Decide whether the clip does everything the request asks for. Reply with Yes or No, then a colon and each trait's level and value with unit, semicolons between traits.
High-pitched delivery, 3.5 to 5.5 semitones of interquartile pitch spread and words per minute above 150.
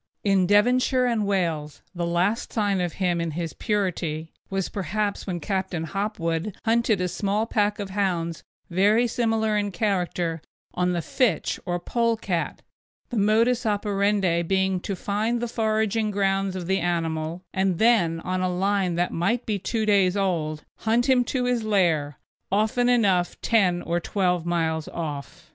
Yes: high, 195 Hz; average, 3.8 semitones; average, 160 wpm